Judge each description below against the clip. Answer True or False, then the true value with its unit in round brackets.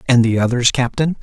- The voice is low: True (125 Hz)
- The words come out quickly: False (195 wpm)